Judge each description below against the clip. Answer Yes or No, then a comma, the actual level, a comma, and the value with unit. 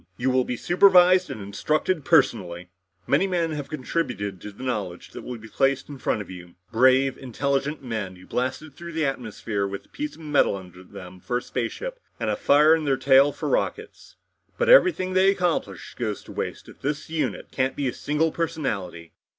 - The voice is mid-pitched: No, low, 130 Hz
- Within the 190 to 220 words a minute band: Yes, average, 195 wpm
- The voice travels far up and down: Yes, wide, 7.2 semitones